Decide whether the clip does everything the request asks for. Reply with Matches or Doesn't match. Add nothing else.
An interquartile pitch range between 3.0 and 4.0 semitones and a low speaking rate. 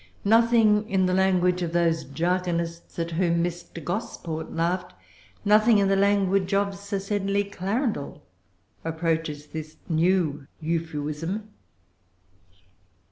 Matches